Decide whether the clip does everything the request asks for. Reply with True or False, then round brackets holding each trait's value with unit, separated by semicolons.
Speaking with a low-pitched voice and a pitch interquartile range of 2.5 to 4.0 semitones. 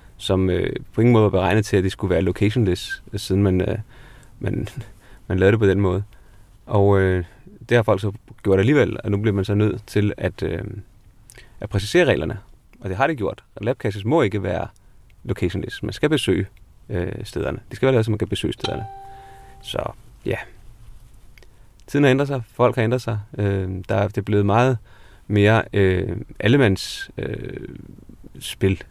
True (105 Hz; 3.3 semitones)